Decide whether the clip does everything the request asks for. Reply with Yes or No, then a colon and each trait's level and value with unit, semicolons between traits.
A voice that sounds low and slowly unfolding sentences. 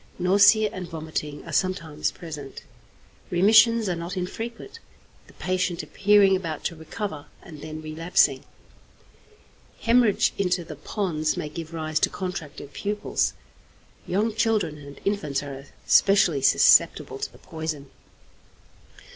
No: medium, 175 Hz; slow, 120 wpm